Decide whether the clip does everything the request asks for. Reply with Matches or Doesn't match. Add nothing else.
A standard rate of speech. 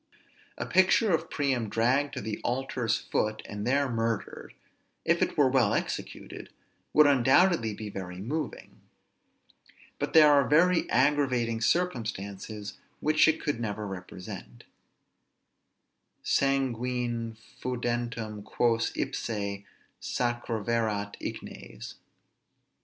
Doesn't match